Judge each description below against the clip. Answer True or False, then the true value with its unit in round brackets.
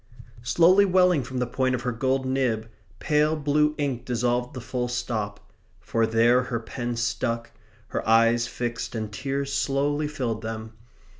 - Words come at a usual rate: True (155 wpm)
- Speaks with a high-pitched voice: False (125 Hz)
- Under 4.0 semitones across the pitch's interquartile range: True (3.0 semitones)